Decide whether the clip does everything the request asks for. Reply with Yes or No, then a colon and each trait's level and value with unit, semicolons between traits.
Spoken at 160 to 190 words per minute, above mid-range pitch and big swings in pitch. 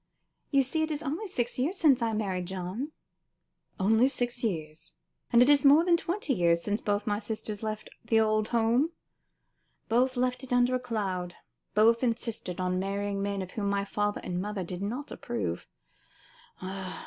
No: average, 170 wpm; high, 220 Hz; average, 4.3 semitones